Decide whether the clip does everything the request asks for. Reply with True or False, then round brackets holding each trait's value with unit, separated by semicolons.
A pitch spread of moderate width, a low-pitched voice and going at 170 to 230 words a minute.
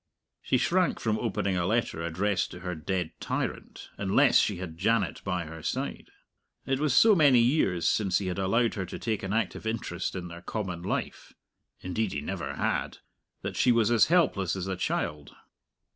True (4.5 semitones; 95 Hz; 185 wpm)